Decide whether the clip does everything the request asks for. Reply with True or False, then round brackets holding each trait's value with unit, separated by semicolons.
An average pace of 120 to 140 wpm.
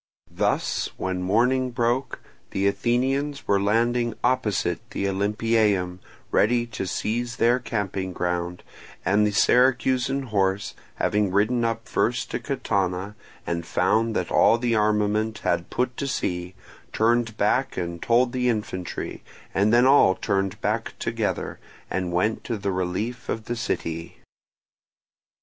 True (135 wpm)